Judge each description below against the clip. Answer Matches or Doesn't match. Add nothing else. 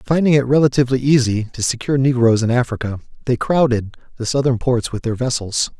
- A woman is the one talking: Doesn't match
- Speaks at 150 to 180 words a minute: Matches